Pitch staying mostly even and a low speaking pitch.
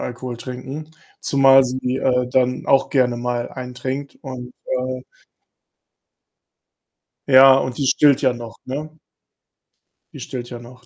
Yes: narrow, 1.3 semitones; low, 130 Hz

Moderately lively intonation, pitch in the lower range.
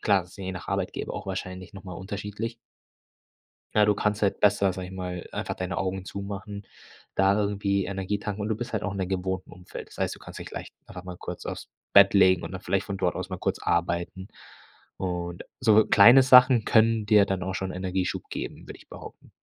No: narrow, 1.9 semitones; very low, 95 Hz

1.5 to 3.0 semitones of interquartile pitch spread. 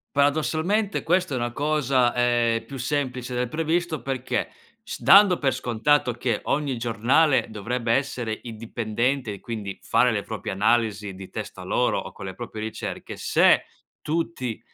No: average, 4.3 semitones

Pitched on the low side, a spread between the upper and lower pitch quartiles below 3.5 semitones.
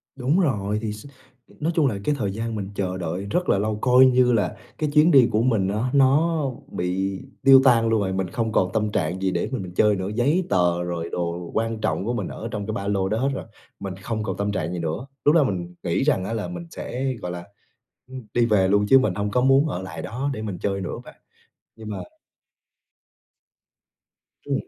No: low, 105 Hz; average, 5.3 semitones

